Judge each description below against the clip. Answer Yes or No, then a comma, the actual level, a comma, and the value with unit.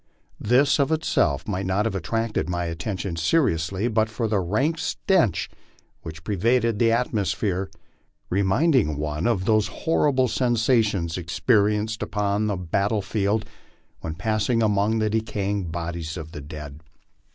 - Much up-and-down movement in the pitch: No, average, 4.6 semitones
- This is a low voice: Yes, low, 105 Hz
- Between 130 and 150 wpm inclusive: Yes, average, 140 wpm